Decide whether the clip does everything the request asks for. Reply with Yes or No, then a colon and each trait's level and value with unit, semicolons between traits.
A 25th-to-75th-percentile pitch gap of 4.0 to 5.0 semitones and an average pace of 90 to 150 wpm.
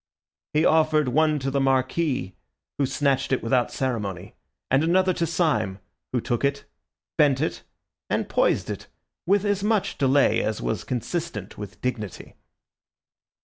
Yes: average, 4.5 semitones; average, 145 wpm